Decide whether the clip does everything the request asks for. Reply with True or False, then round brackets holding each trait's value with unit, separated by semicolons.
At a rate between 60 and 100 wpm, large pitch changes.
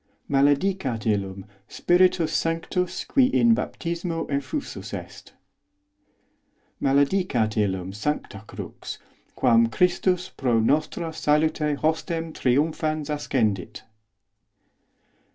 True (95 wpm; 6.3 semitones)